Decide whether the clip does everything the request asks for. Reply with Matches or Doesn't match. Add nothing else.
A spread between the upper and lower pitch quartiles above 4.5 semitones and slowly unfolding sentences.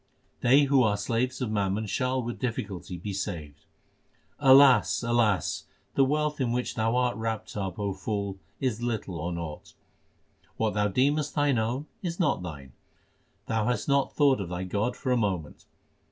Doesn't match